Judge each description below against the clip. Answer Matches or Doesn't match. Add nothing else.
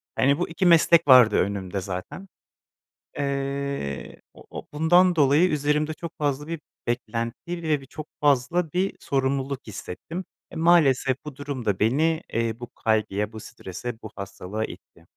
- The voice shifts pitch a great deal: Matches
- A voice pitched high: Doesn't match